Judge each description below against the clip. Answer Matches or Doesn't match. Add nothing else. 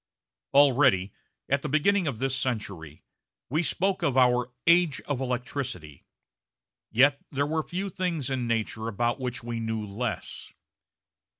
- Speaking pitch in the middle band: Doesn't match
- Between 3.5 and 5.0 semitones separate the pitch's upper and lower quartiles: Matches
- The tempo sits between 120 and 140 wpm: Matches